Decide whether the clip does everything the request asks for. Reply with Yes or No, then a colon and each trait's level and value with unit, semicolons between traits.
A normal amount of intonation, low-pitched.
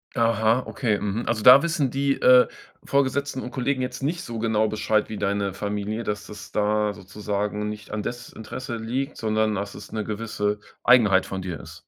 Yes: average, 3.2 semitones; low, 110 Hz